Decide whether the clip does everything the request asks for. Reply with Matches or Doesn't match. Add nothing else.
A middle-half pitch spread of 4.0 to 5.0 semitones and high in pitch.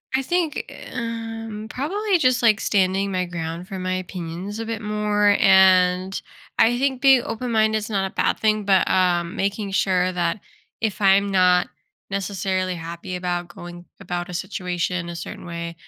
Doesn't match